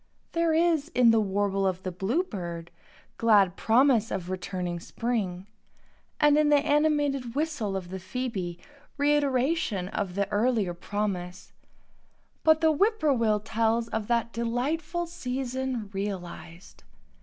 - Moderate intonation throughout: No, wide, 7.0 semitones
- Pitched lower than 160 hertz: No, high, 230 Hz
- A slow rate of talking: Yes, slow, 120 wpm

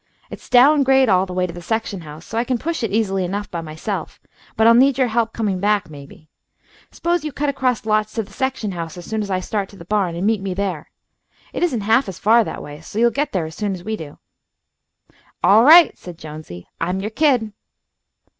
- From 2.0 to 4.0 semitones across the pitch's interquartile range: No, average, 4.8 semitones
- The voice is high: Yes, high, 210 Hz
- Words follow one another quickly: Yes, fast, 230 wpm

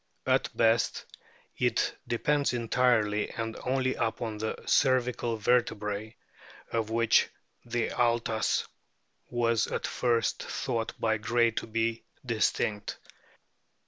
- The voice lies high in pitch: No, low, 115 Hz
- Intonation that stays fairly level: Yes, narrow, 1.5 semitones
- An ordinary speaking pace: No, slow, 105 wpm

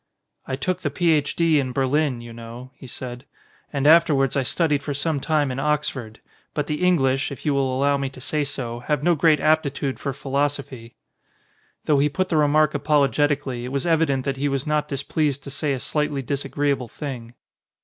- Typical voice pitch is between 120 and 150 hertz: Yes, medium, 140 Hz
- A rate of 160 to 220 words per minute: Yes, average, 190 wpm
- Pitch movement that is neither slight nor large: No, narrow, 2.3 semitones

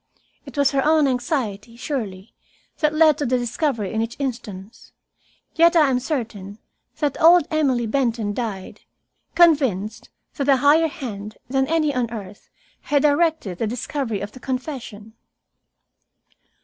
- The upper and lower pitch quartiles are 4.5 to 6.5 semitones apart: Yes, average, 5.1 semitones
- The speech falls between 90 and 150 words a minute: Yes, average, 140 wpm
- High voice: Yes, very high, 255 Hz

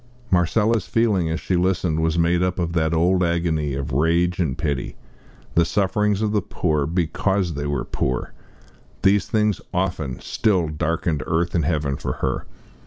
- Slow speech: No, average, 165 wpm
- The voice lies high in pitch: No, very low, 85 Hz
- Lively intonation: No, average, 3.3 semitones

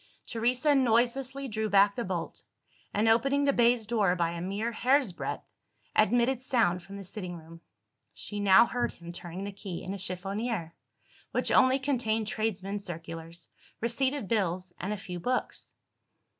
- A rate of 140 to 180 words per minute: Yes, average, 155 wpm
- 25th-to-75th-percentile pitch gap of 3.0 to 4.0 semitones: No, average, 4.8 semitones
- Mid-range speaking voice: No, high, 210 Hz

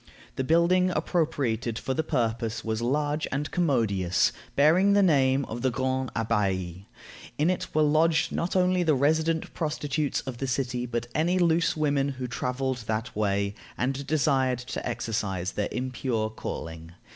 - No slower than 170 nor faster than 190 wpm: No, average, 155 wpm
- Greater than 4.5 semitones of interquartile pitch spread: Yes, average, 5.2 semitones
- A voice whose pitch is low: Yes, low, 130 Hz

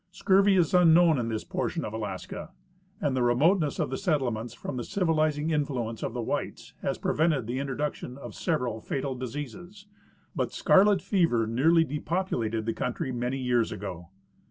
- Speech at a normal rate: Yes, average, 165 wpm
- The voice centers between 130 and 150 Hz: Yes, low, 135 Hz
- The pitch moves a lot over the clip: Yes, wide, 5.8 semitones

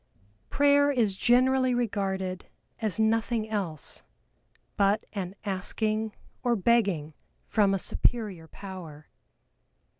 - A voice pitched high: Yes, high, 210 Hz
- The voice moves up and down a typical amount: Yes, average, 3.8 semitones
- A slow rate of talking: Yes, slow, 95 wpm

